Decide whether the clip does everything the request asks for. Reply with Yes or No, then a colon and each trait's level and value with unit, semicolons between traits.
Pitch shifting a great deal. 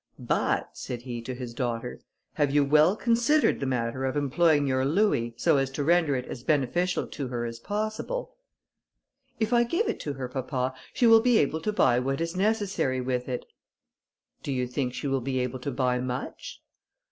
Yes: wide, 5.7 semitones